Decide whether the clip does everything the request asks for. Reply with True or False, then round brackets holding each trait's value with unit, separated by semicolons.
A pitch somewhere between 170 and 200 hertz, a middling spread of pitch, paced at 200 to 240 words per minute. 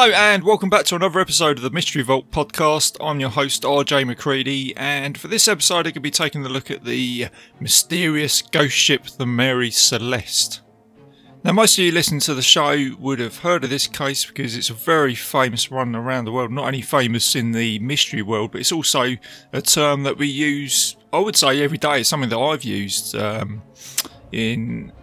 False (135 Hz; 4.0 semitones; 205 wpm)